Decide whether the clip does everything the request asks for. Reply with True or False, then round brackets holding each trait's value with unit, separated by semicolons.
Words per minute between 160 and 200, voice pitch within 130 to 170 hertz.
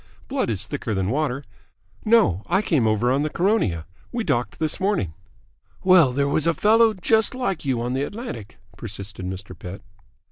True (180 wpm; 140 Hz)